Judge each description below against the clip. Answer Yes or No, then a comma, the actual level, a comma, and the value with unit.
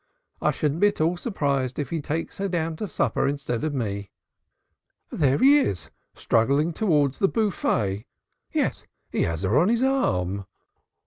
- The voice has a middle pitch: Yes, medium, 145 Hz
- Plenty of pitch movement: Yes, wide, 7.6 semitones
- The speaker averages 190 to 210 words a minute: No, average, 165 wpm